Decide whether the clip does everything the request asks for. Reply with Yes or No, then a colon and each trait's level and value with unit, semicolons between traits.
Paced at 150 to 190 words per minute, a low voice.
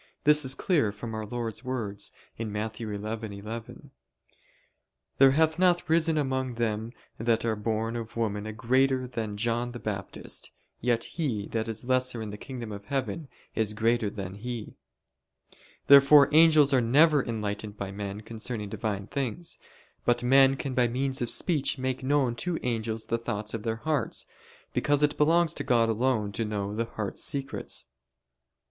Yes: average, 160 wpm; low, 115 Hz